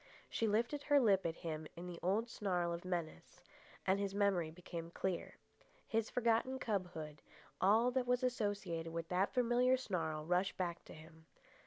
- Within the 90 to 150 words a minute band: No, average, 165 wpm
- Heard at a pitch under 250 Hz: Yes, high, 190 Hz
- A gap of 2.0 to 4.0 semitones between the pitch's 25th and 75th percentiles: No, average, 5.2 semitones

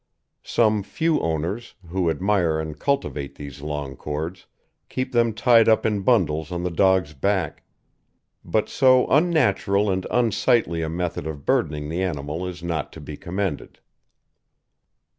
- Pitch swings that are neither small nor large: No, wide, 5.8 semitones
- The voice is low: Yes, very low, 90 Hz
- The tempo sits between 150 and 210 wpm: No, average, 140 wpm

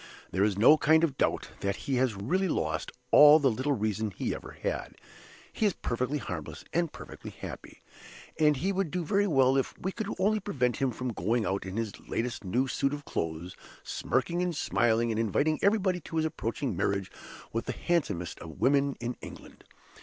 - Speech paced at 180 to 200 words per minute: Yes, average, 190 wpm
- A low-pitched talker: Yes, low, 130 Hz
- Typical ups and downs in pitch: No, wide, 6.4 semitones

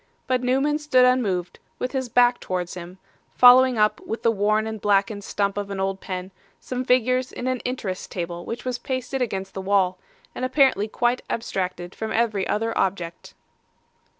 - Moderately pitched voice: No, high, 220 Hz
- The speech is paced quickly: No, average, 175 wpm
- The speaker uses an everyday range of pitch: Yes, average, 4.6 semitones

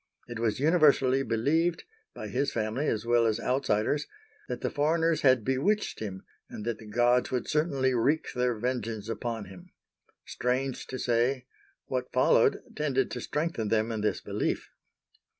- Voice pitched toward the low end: Yes, low, 125 Hz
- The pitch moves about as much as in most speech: Yes, average, 4.1 semitones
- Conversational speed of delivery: Yes, average, 150 wpm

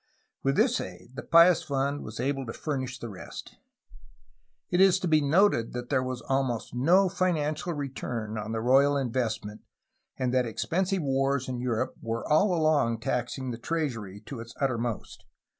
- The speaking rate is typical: Yes, average, 165 wpm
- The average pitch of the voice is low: Yes, low, 130 Hz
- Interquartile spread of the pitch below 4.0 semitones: No, average, 4.7 semitones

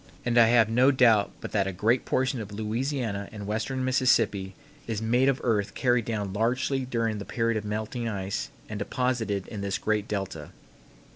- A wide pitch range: No, average, 3.2 semitones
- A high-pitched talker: No, low, 110 Hz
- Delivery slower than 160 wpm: No, average, 185 wpm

